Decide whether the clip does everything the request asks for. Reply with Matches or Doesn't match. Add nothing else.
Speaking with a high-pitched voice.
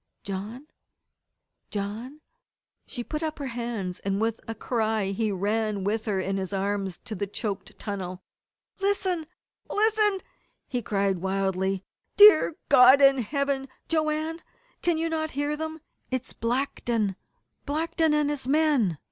Matches